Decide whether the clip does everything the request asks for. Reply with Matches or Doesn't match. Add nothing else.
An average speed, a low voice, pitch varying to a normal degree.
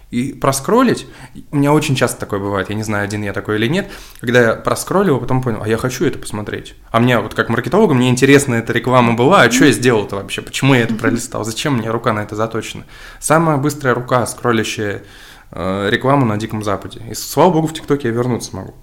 Doesn't match